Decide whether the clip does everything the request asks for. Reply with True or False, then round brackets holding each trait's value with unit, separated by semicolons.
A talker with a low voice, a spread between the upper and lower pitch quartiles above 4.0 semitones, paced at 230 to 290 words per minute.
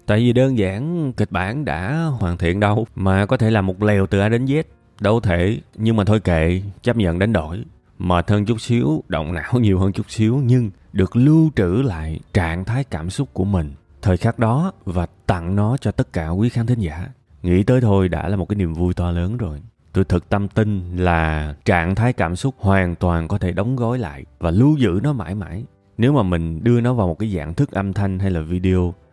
True (100 Hz; 4.6 semitones; 235 wpm)